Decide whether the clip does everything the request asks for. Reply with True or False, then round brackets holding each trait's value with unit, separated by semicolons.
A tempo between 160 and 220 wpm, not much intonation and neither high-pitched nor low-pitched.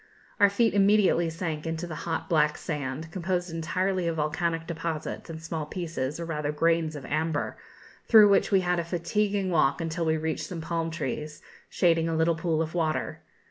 True (180 wpm; 2.0 semitones; 165 Hz)